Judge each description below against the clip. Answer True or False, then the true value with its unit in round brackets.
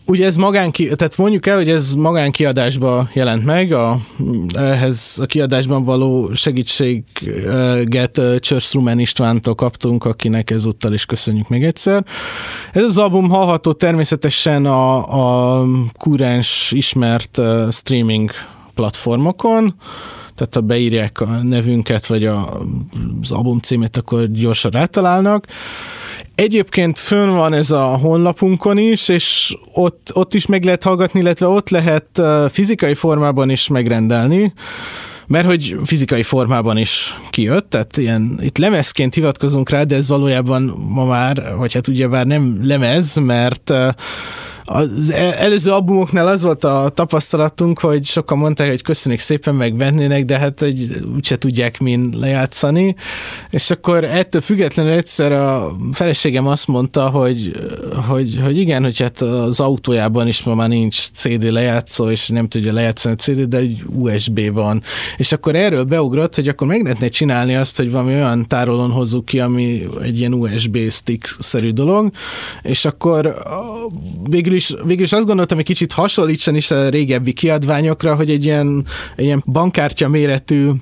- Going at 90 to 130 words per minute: False (145 wpm)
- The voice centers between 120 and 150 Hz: True (135 Hz)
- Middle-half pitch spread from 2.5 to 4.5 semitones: False (5.0 semitones)